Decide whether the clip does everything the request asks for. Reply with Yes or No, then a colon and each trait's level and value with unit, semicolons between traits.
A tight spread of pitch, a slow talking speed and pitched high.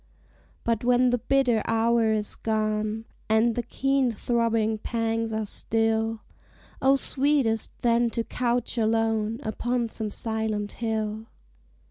Yes: narrow, 1.6 semitones; slow, 120 wpm; high, 225 Hz